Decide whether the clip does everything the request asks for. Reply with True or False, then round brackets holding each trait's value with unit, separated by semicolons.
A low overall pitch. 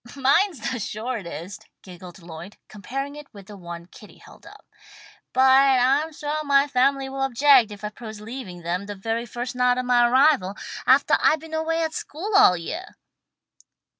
False (250 Hz)